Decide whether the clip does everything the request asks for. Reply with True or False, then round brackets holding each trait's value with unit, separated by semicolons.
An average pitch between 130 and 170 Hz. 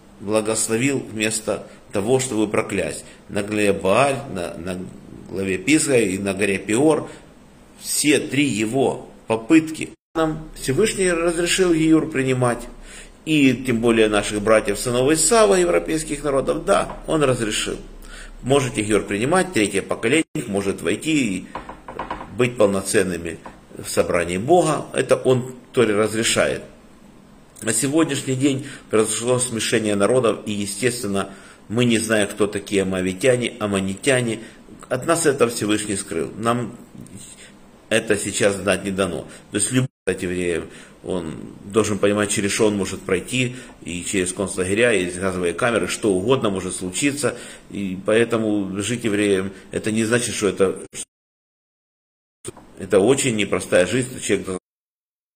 False (110 Hz)